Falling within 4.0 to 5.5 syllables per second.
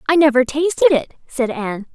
No: 5.8 syllables/s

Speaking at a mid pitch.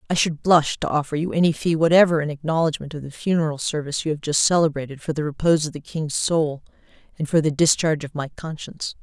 Yes: medium, 155 Hz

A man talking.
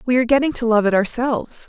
No: female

